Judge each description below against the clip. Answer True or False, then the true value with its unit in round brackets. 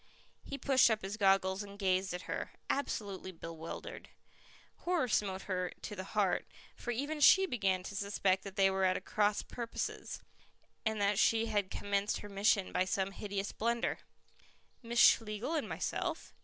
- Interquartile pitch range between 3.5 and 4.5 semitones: False (2.9 semitones)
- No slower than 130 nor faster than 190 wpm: True (160 wpm)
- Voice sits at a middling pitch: False (200 Hz)